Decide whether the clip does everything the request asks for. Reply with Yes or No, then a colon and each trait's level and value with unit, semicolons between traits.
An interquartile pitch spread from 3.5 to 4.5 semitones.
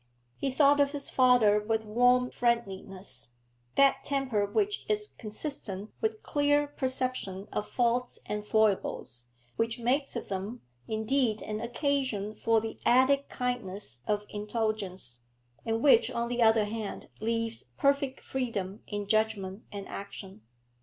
Yes: average, 3.9 semitones